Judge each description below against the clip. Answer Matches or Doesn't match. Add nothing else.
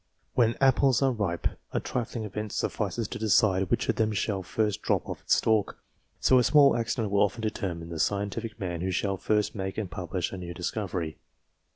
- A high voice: Doesn't match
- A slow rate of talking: Doesn't match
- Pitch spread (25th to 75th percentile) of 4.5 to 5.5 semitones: Doesn't match